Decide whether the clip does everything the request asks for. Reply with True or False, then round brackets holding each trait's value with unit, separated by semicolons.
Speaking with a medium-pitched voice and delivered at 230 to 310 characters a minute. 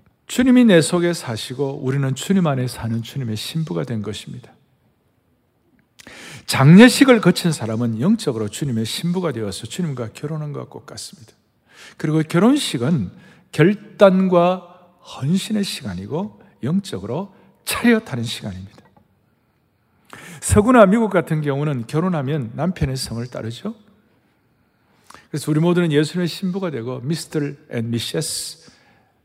True (155 Hz; 285 characters per minute)